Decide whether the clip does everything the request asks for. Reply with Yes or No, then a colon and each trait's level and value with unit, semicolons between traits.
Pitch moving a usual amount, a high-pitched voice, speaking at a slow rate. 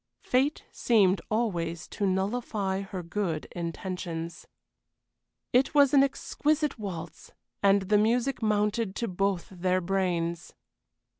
Yes: average, 4.5 semitones; high, 195 Hz; slow, 115 wpm